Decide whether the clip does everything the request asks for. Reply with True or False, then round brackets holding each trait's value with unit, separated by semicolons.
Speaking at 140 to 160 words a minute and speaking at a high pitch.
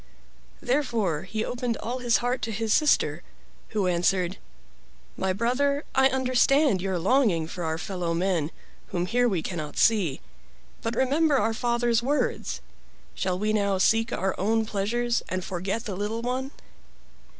True (150 wpm; 220 Hz)